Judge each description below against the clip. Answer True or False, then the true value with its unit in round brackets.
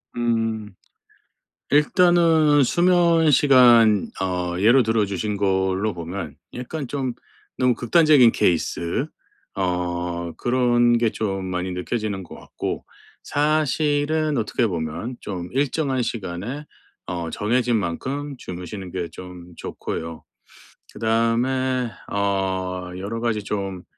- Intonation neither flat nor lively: False (6.0 semitones)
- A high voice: False (110 Hz)